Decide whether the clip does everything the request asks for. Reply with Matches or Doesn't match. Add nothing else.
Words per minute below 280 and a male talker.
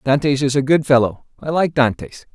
Matches